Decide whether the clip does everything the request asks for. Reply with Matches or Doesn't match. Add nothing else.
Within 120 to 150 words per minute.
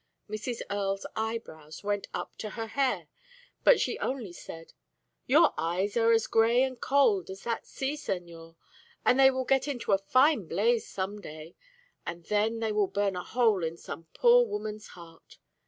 Doesn't match